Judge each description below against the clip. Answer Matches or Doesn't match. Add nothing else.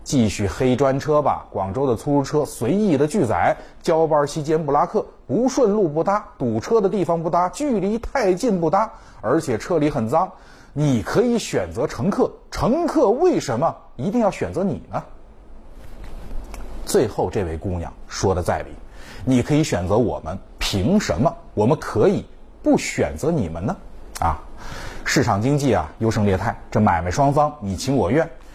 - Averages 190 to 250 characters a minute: Matches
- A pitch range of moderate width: Doesn't match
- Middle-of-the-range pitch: Matches